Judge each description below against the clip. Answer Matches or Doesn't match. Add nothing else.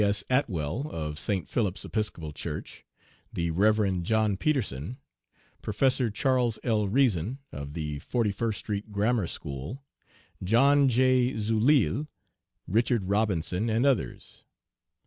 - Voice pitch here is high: Doesn't match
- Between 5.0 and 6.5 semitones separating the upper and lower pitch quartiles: Matches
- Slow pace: Matches